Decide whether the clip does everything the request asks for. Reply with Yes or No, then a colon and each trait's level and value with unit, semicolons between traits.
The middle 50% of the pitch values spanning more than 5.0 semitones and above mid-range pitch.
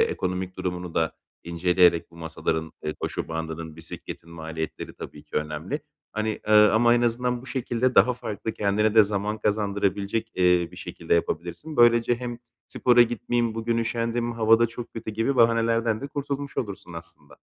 No: wide, 5.6 semitones; low, 110 Hz